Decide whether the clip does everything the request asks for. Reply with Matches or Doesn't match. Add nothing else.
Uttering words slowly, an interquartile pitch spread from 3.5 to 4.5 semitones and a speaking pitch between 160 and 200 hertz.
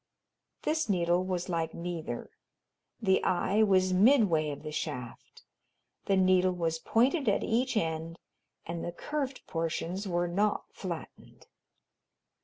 Matches